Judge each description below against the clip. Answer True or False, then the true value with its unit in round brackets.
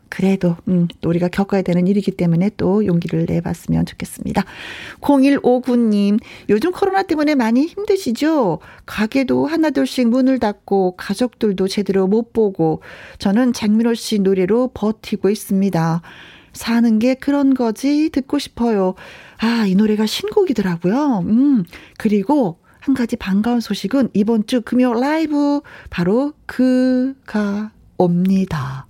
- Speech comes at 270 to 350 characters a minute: True (280 characters per minute)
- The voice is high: True (220 Hz)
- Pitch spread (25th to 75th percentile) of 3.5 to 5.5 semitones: True (5.1 semitones)